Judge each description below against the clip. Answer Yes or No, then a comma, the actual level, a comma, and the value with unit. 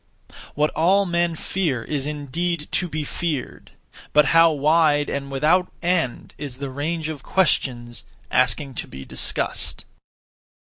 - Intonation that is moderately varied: Yes, average, 3.5 semitones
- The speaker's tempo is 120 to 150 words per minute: Yes, slow, 135 wpm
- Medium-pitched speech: Yes, medium, 150 Hz